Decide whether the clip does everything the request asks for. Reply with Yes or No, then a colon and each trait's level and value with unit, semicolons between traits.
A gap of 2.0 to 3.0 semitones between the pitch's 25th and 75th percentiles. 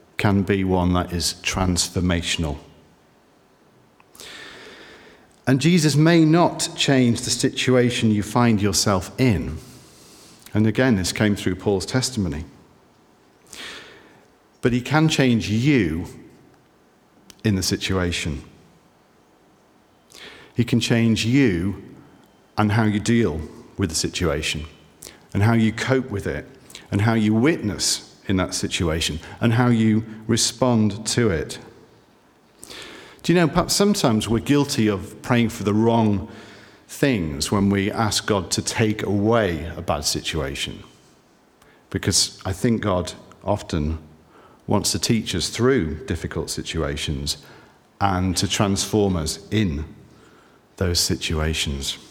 No: average, 5.1 semitones